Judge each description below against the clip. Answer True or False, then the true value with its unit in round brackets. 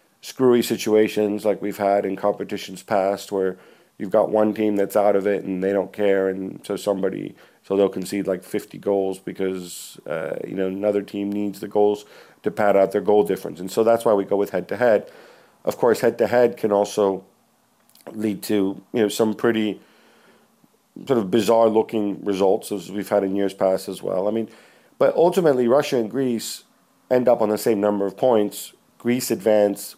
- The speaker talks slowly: False (195 wpm)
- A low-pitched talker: True (105 Hz)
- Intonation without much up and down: True (1.7 semitones)